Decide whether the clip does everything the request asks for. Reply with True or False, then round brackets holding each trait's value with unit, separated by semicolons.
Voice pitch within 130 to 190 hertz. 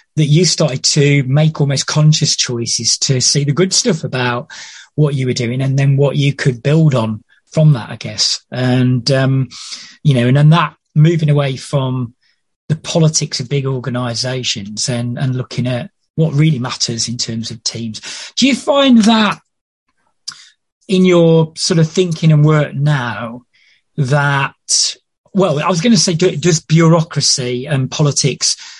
True (140 Hz)